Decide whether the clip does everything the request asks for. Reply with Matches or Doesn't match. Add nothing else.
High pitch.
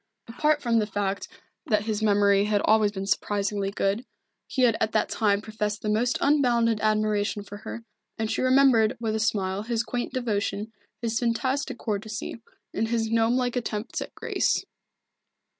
Matches